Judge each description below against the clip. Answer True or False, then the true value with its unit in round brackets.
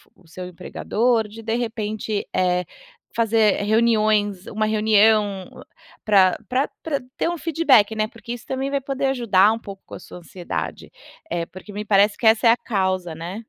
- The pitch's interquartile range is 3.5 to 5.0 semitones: False (3.0 semitones)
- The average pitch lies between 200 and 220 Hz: True (215 Hz)